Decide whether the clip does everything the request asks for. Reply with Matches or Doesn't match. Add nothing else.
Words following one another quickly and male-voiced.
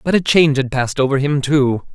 Matches